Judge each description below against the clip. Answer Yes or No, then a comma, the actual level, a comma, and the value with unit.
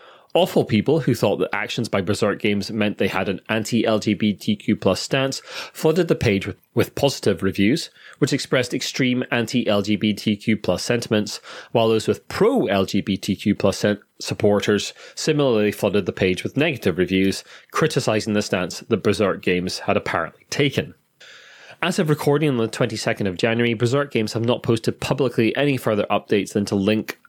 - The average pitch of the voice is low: Yes, low, 110 Hz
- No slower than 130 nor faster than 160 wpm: Yes, average, 155 wpm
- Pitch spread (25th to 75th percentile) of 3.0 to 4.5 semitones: Yes, average, 3.4 semitones